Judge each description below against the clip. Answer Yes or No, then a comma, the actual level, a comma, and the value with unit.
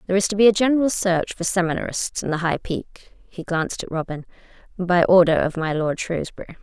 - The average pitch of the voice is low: No, medium, 180 Hz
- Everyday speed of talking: No, fast, 210 wpm